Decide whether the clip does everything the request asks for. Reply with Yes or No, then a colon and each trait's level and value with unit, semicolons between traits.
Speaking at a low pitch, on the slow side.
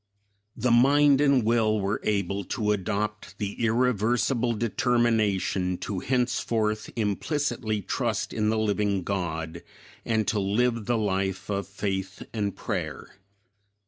Yes: low, 105 Hz; slow, 120 wpm